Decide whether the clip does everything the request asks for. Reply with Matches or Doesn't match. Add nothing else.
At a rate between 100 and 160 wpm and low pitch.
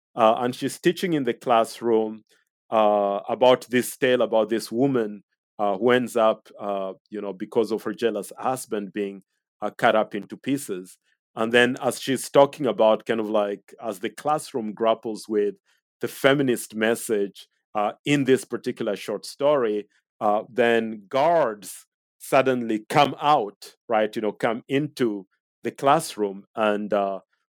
Matches